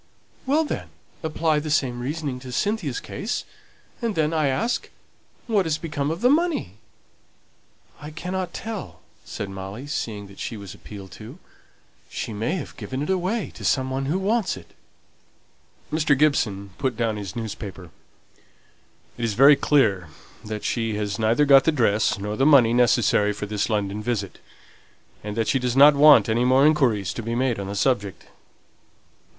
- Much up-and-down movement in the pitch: Yes, wide, 6.4 semitones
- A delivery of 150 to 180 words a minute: Yes, average, 165 wpm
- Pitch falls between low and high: No, low, 125 Hz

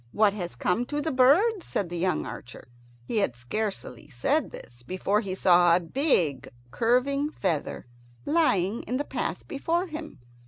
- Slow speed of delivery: No, average, 160 wpm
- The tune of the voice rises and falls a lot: Yes, wide, 8.5 semitones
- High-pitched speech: Yes, high, 210 Hz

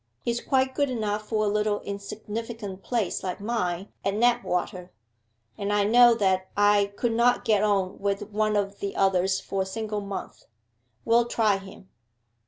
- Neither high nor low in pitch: No, high, 205 Hz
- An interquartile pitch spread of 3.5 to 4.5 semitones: No, narrow, 2.5 semitones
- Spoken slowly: No, average, 165 wpm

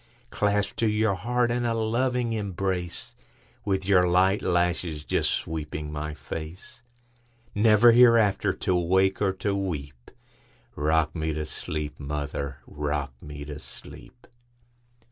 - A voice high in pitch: No, very low, 95 Hz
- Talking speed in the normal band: No, slow, 110 wpm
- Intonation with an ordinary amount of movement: No, wide, 6.2 semitones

